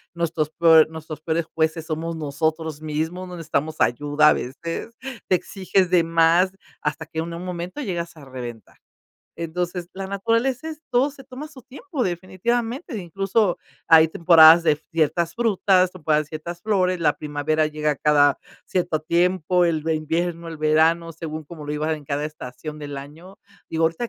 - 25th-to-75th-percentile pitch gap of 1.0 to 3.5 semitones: Yes, average, 2.9 semitones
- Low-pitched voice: No, medium, 165 Hz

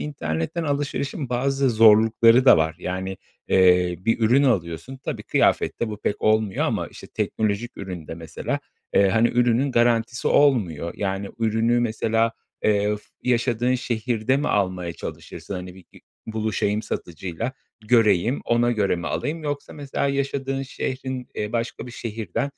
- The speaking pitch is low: Yes, low, 115 Hz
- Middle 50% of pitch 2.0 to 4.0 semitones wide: No, average, 4.6 semitones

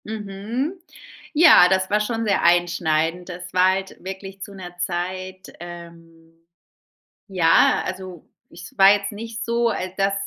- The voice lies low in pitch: No, medium, 185 Hz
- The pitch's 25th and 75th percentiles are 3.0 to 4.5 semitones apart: No, narrow, 2.6 semitones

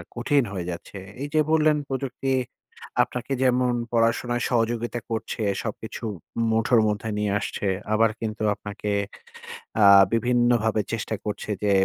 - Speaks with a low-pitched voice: Yes, low, 115 Hz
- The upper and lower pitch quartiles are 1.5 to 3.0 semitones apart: Yes, narrow, 2.4 semitones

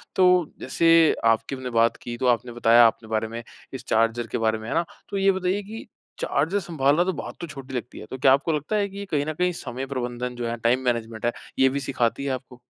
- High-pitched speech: No, low, 130 Hz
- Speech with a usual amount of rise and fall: No, wide, 5.9 semitones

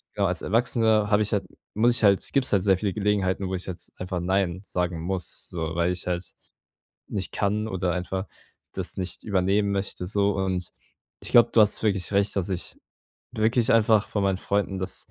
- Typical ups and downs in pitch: No, narrow, 2.3 semitones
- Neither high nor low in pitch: No, very low, 95 Hz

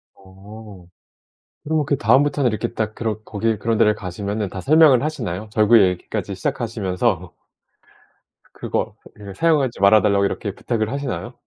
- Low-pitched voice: Yes, low, 110 Hz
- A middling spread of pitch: Yes, average, 4.0 semitones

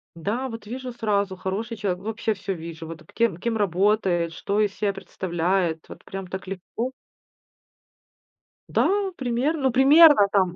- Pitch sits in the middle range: No, high, 200 Hz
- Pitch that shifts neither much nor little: Yes, average, 4.0 semitones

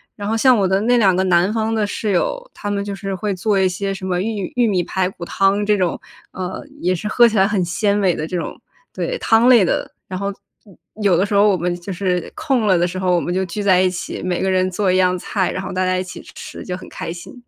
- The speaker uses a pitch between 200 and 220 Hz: No, high, 190 Hz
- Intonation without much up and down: Yes, narrow, 2.3 semitones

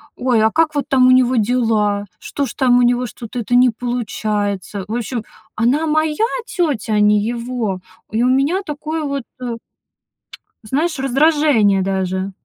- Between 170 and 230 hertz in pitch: No, high, 245 Hz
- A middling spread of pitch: Yes, average, 4.6 semitones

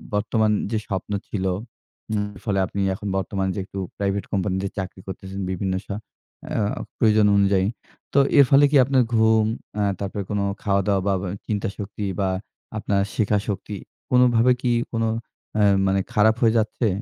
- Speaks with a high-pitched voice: No, low, 105 Hz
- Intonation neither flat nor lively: No, narrow, 2.2 semitones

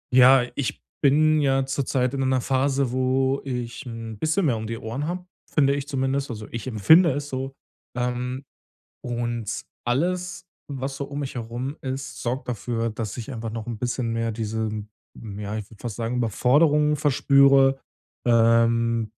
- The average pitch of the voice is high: No, low, 125 Hz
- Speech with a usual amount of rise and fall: Yes, average, 3.1 semitones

